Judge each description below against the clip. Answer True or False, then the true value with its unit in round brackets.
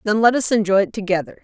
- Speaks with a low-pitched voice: False (210 Hz)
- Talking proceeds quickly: True (250 wpm)